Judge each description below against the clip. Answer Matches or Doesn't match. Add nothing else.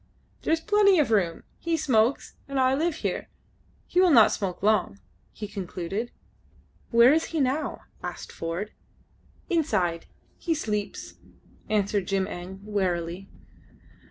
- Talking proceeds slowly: Matches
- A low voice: Doesn't match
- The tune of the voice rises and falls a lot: Matches